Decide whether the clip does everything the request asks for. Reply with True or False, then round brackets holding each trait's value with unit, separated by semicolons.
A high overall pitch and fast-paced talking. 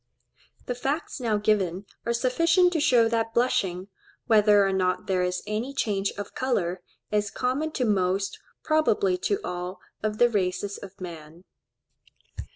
False (210 Hz; 150 wpm)